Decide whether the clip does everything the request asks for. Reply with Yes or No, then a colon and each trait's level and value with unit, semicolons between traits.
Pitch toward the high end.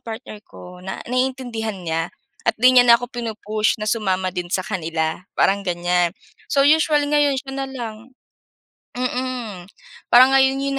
Yes: high, 225 Hz